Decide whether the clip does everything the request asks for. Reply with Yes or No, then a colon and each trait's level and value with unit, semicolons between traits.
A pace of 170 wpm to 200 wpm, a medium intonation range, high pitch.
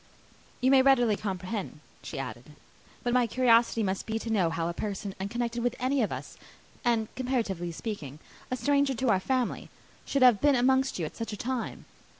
Yes: average, 185 wpm; average, 4.4 semitones; high, 235 Hz